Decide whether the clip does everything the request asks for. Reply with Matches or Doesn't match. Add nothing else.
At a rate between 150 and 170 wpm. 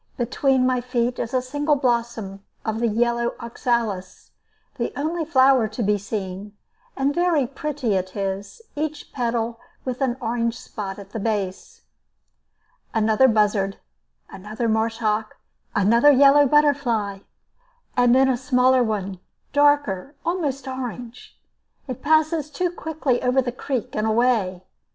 Doesn't match